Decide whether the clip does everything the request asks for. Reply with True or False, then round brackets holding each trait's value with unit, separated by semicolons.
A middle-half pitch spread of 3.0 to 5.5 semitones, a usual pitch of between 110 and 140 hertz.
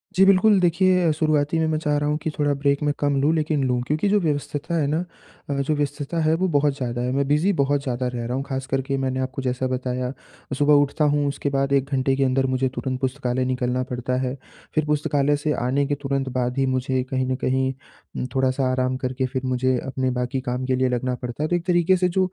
False (2.6 semitones; 135 Hz)